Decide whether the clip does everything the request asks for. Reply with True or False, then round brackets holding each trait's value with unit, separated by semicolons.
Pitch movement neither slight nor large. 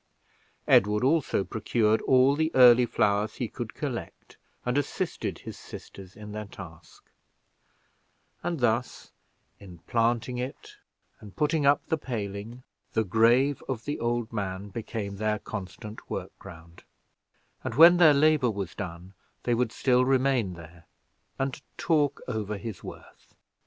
True (4.4 semitones)